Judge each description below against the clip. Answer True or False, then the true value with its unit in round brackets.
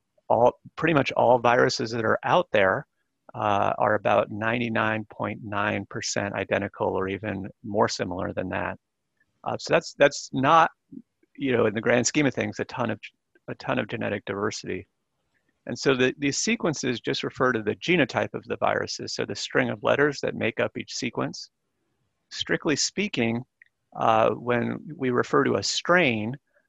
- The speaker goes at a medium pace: True (165 wpm)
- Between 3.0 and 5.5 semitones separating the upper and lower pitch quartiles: True (3.5 semitones)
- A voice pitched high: False (115 Hz)